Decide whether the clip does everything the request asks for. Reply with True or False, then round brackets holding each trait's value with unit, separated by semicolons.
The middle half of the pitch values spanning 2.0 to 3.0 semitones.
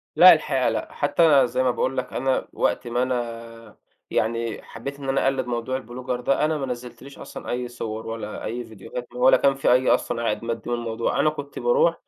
True (2.5 semitones)